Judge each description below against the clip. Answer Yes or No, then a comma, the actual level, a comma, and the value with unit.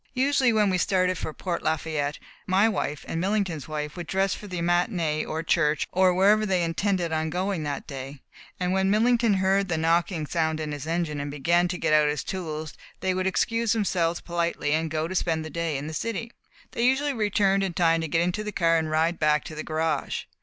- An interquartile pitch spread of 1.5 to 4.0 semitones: Yes, average, 3.5 semitones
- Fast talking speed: Yes, fast, 215 wpm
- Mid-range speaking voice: Yes, medium, 175 Hz